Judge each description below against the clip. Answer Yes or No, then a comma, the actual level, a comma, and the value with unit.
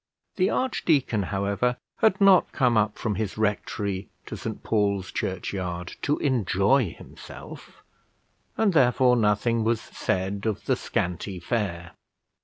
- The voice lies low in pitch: Yes, low, 105 Hz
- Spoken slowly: Yes, slow, 125 wpm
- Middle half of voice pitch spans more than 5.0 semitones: No, average, 4.4 semitones